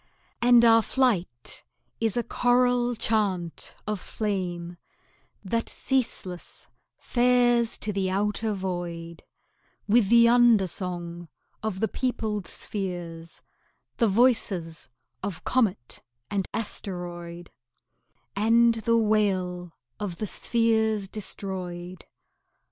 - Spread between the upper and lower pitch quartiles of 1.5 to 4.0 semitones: No, average, 4.5 semitones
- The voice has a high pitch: Yes, high, 205 Hz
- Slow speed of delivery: Yes, slow, 95 wpm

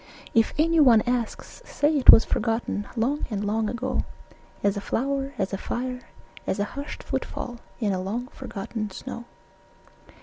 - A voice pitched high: Yes, high, 235 Hz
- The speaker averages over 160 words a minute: No, average, 155 wpm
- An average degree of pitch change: Yes, average, 4.0 semitones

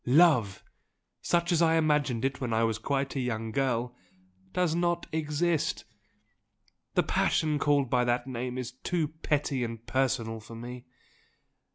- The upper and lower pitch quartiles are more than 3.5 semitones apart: Yes, average, 4.5 semitones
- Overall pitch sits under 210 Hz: Yes, low, 135 Hz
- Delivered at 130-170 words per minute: Yes, average, 150 wpm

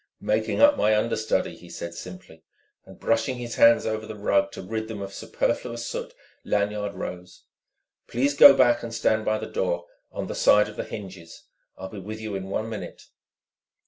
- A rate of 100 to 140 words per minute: No, average, 185 wpm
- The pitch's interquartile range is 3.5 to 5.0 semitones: No, average, 2.8 semitones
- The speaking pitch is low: Yes, low, 110 Hz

